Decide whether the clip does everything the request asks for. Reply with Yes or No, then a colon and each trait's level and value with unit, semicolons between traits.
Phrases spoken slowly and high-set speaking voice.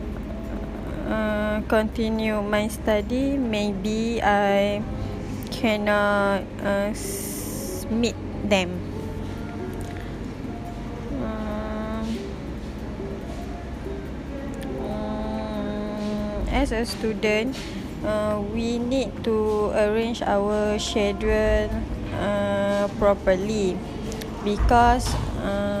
Yes: slow, 60 wpm; high, 205 Hz